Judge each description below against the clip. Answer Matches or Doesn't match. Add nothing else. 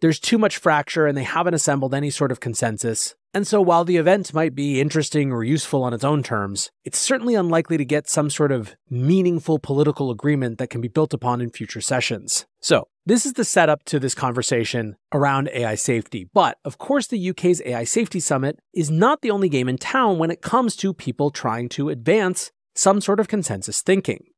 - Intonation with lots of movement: Matches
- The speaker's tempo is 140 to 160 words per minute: Doesn't match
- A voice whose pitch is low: Doesn't match